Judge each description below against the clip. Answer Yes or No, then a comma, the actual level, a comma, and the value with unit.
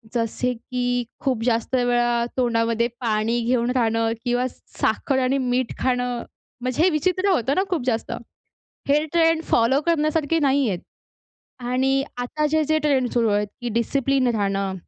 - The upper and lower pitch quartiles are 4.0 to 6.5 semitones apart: No, average, 3.2 semitones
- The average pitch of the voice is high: Yes, very high, 250 Hz